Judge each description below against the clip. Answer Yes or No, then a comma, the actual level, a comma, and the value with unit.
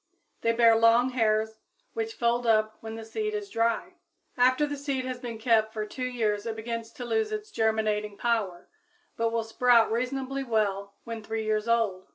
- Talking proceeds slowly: No, average, 185 wpm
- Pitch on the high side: Yes, high, 230 Hz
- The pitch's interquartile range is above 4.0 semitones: No, narrow, 2.5 semitones